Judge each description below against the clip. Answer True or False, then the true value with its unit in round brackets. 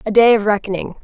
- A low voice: False (210 Hz)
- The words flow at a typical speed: False (235 wpm)